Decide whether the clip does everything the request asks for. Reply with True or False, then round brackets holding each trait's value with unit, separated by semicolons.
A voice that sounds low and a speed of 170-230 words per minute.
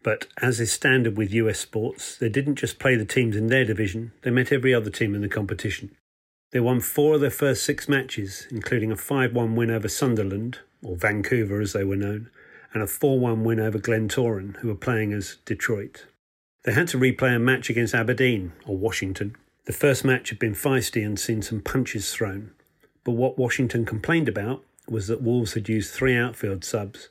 True (115 Hz; 200 wpm)